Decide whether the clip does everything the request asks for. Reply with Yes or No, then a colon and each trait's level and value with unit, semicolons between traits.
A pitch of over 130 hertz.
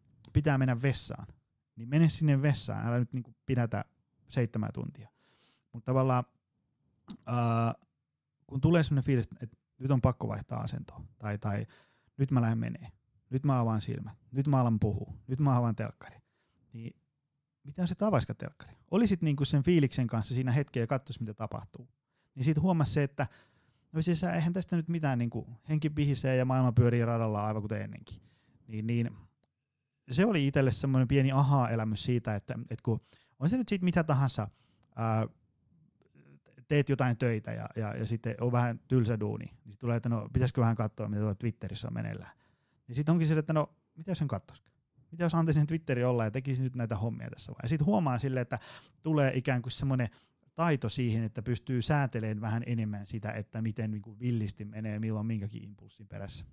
No: low, 125 Hz